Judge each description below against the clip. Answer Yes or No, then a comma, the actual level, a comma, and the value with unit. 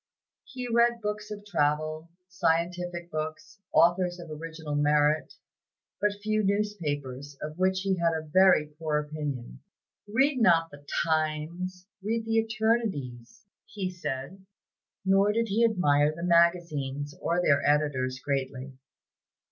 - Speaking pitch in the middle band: Yes, medium, 170 Hz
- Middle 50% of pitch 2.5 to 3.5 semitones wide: No, average, 4.9 semitones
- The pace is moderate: No, slow, 125 wpm